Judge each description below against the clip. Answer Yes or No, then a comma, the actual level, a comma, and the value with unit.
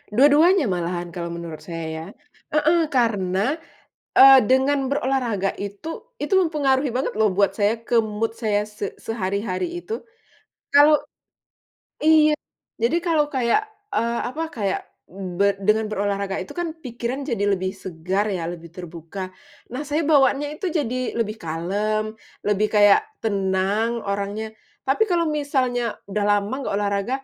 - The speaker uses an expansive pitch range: Yes, wide, 5.7 semitones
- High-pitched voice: Yes, high, 215 Hz